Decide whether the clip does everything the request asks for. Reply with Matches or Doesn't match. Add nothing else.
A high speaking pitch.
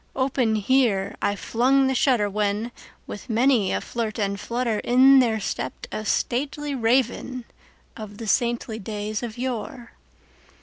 Matches